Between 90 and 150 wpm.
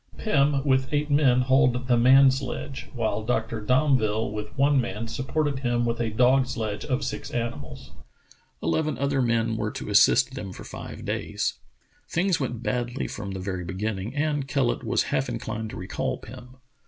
No: average, 170 wpm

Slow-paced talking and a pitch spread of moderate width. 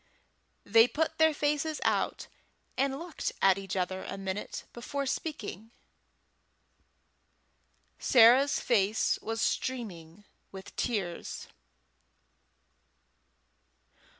No: slow, 85 wpm; wide, 6.3 semitones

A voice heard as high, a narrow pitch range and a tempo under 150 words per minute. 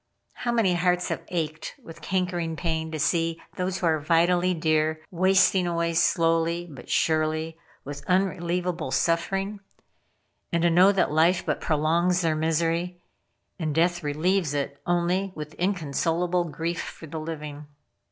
No: medium, 170 Hz; narrow, 2.3 semitones; average, 140 wpm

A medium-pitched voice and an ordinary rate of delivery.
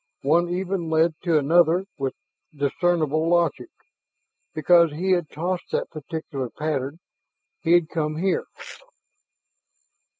No: medium, 165 Hz; slow, 110 wpm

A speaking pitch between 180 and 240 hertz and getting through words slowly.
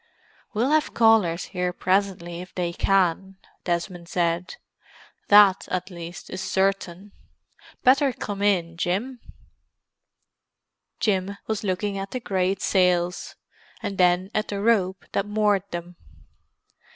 Yes: high, 190 Hz; slow, 120 wpm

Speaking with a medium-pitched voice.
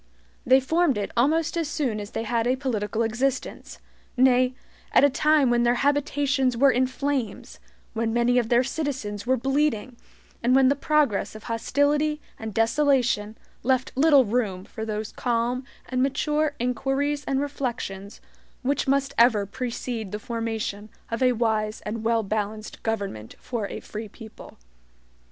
No: high, 245 Hz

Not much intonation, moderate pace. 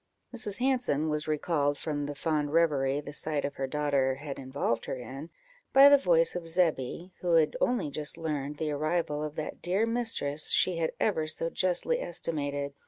No: average, 3.4 semitones; average, 180 wpm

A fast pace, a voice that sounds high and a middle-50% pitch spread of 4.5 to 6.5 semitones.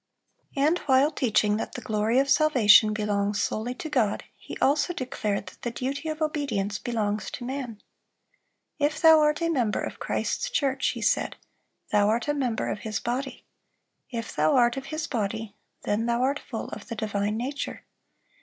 No: average, 180 wpm; high, 245 Hz; average, 5.0 semitones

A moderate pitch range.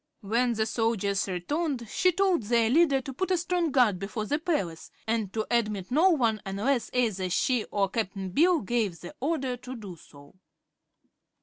No: wide, 5.9 semitones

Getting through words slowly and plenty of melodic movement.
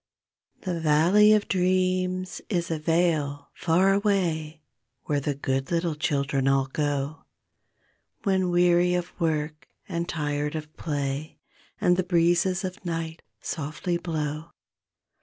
No: slow, 125 wpm; average, 3.2 semitones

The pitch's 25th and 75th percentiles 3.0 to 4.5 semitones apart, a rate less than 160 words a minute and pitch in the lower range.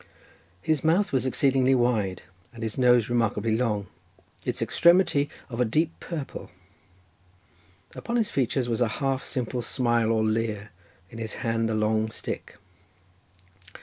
Yes: average, 3.3 semitones; average, 145 wpm; low, 120 Hz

